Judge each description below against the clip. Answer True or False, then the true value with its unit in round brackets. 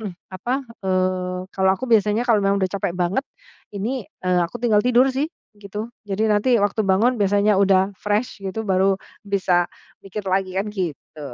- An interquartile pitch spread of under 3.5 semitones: True (2.4 semitones)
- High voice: True (195 Hz)